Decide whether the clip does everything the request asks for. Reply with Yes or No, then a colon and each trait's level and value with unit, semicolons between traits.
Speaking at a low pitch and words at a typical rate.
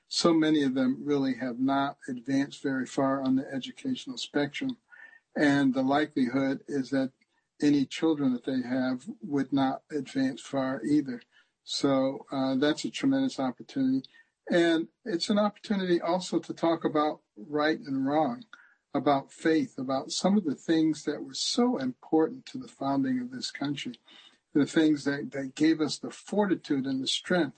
No: medium, 155 Hz; average, 160 wpm